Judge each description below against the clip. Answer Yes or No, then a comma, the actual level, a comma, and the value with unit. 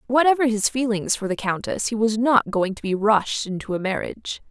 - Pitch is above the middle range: Yes, high, 220 Hz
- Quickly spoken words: Yes, fast, 215 wpm